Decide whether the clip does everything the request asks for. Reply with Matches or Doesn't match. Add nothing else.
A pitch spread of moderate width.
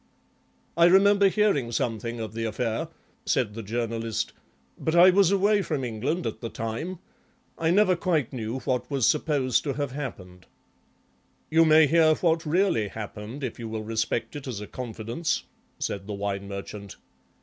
Doesn't match